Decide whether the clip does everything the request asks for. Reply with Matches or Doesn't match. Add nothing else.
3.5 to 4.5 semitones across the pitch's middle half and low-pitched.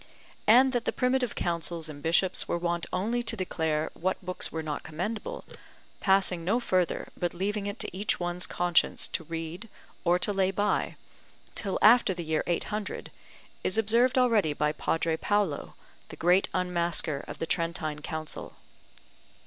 Doesn't match